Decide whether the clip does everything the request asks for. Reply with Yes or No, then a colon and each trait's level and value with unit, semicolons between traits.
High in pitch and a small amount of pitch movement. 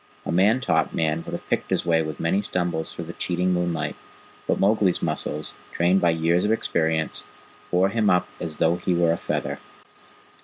No: very low, 85 Hz; narrow, 2.1 semitones